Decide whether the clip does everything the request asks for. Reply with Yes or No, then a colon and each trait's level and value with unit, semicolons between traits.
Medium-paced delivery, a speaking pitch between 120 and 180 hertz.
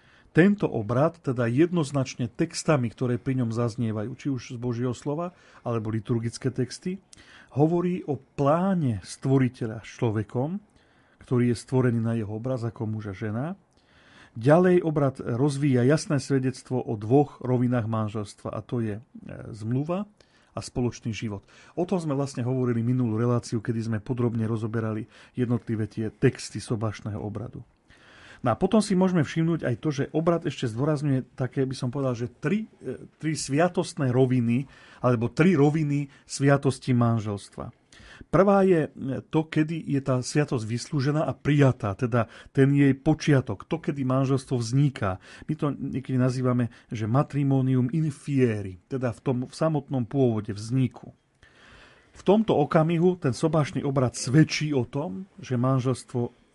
Yes: average, 140 wpm; low, 130 Hz